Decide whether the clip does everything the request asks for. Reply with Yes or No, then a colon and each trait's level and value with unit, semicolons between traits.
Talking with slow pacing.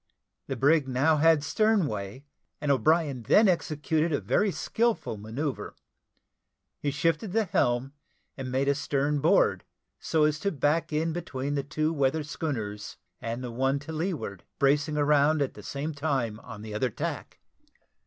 No: average, 160 wpm